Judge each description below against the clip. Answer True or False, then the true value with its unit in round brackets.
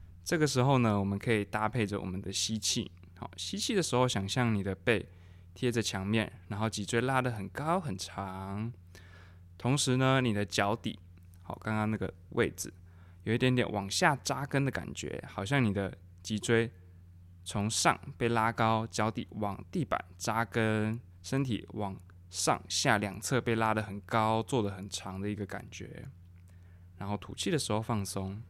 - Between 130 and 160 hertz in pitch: False (105 Hz)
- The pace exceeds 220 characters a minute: True (240 characters per minute)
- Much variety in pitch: False (4.0 semitones)